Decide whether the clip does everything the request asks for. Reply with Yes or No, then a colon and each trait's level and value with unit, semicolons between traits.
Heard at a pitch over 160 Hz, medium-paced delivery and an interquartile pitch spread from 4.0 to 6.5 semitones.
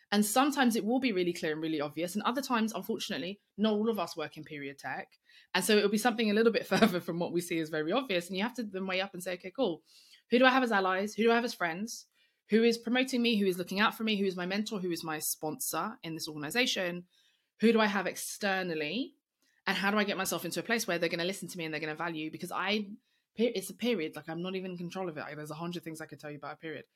No: high, 190 Hz; fast, 295 wpm; average, 4.8 semitones